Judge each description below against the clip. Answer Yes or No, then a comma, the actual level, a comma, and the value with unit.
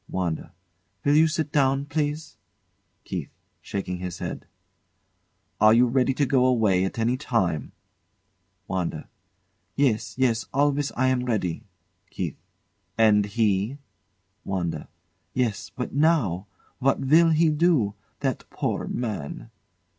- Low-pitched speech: Yes, low, 125 Hz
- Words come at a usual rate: No, slow, 120 wpm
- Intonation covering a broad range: Yes, wide, 6.2 semitones